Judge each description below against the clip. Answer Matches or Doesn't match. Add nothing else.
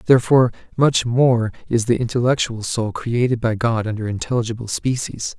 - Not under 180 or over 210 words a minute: Doesn't match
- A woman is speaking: Doesn't match